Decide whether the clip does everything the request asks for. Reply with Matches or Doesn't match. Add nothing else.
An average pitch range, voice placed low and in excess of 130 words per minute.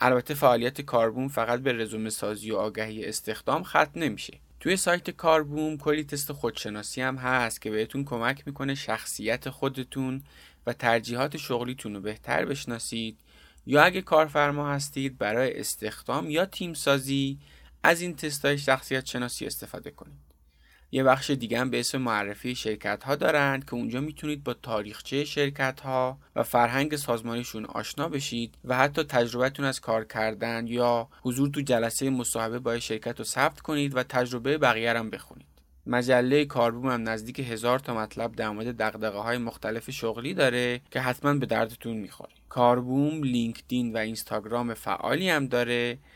Matches